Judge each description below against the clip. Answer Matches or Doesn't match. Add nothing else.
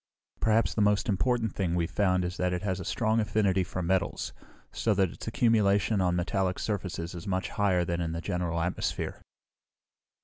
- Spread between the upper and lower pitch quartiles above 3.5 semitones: Doesn't match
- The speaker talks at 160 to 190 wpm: Matches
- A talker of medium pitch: Doesn't match